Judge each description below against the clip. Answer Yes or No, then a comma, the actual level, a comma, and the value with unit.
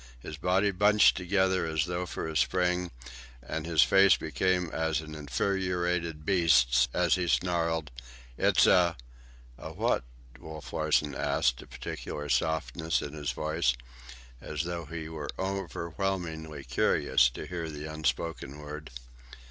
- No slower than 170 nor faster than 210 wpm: No, slow, 135 wpm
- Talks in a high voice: No, very low, 80 Hz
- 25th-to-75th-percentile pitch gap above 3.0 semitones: No, average, 2.7 semitones